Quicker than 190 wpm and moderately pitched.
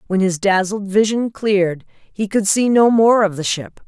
No: average, 200 wpm; high, 200 Hz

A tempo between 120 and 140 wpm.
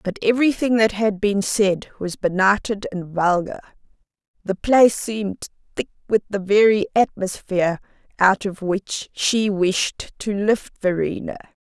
Yes: slow, 135 wpm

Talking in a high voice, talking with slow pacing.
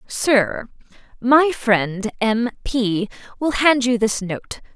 Yes: high, 230 Hz; slow, 115 wpm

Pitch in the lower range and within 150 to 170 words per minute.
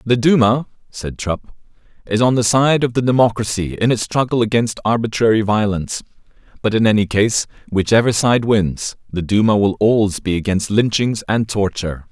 Yes: low, 110 Hz; average, 165 wpm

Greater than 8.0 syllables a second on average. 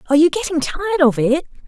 Yes: 8.3 syllables/s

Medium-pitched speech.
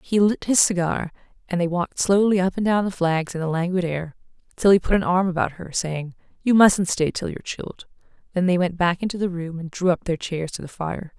Yes: medium, 180 Hz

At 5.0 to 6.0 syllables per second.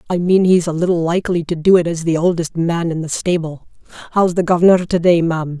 Yes: 5.9 syllables/s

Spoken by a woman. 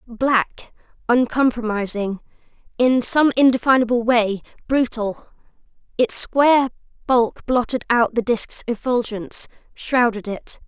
Yes: female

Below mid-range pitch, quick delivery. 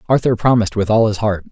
Yes: low, 110 Hz; fast, 235 wpm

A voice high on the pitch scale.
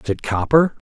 No: low, 130 Hz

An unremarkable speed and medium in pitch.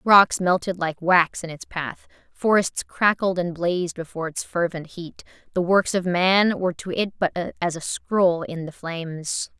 Yes: average, 180 wpm; medium, 175 Hz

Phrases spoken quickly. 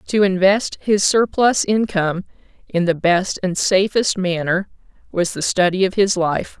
No: average, 155 wpm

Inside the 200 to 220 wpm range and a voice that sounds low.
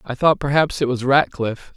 Yes: fast, 205 wpm; low, 130 Hz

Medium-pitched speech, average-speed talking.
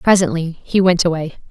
Yes: medium, 175 Hz; average, 160 wpm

